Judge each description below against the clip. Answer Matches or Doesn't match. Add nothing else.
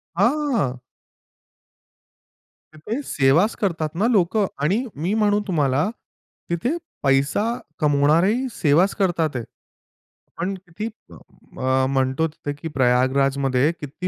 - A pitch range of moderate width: Doesn't match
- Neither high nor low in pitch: Matches